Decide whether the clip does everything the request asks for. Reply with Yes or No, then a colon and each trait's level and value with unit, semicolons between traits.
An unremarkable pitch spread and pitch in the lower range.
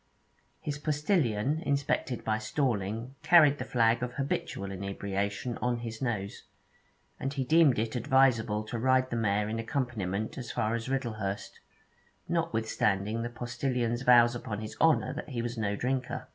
Yes: average, 3.6 semitones; low, 120 Hz